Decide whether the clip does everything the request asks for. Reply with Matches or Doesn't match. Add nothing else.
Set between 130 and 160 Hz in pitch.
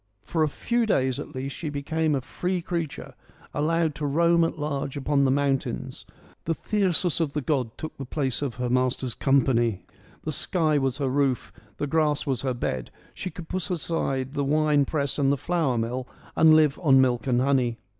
Matches